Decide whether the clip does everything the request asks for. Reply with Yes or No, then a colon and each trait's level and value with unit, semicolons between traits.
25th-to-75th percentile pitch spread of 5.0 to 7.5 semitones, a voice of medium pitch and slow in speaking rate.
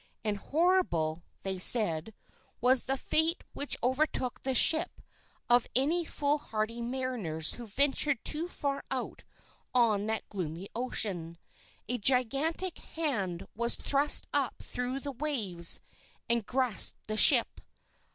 No: wide, 5.5 semitones; high, 245 Hz; slow, 120 wpm